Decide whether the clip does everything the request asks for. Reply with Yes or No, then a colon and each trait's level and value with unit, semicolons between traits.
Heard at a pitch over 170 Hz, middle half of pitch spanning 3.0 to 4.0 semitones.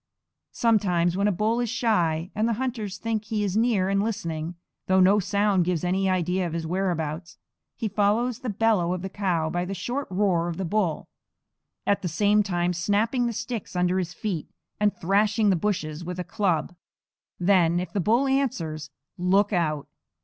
Yes: high, 190 Hz; average, 3.3 semitones